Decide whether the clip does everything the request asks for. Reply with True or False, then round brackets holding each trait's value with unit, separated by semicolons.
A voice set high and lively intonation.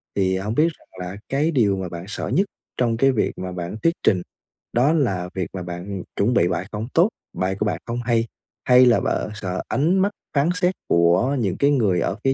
False (110 Hz; 6.7 semitones)